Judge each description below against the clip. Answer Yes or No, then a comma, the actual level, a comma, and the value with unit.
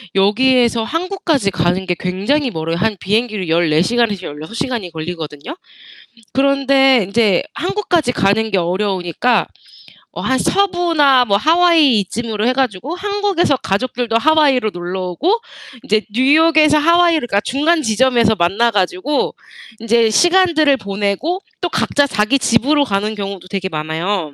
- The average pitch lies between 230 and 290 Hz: Yes, high, 235 Hz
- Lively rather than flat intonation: Yes, wide, 7.1 semitones